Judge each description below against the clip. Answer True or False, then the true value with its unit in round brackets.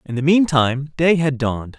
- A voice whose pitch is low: False (145 Hz)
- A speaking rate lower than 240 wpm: True (200 wpm)